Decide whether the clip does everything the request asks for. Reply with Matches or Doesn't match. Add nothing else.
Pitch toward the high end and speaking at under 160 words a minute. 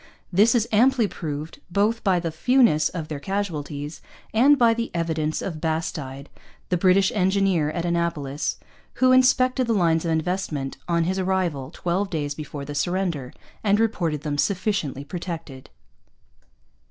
Doesn't match